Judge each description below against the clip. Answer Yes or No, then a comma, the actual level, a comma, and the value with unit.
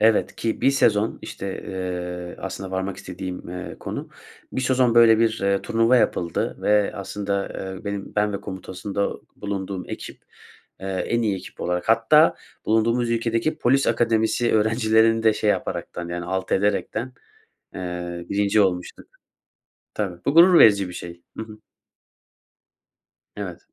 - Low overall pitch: Yes, low, 105 Hz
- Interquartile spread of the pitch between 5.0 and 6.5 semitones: No, average, 3.3 semitones